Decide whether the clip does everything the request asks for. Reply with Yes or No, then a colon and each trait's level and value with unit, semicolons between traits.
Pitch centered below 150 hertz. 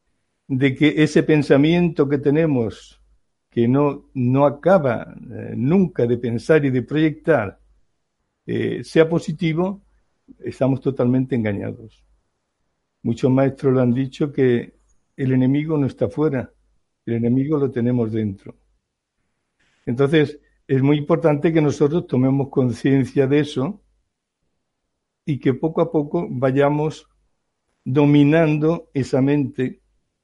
Yes: low, 135 Hz